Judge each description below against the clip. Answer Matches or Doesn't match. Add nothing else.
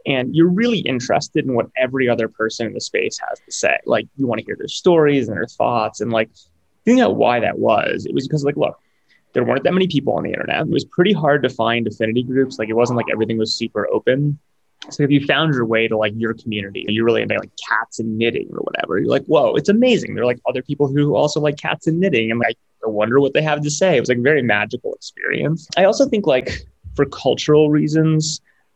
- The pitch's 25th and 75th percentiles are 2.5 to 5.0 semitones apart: Doesn't match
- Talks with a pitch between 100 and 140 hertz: Matches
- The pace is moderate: Doesn't match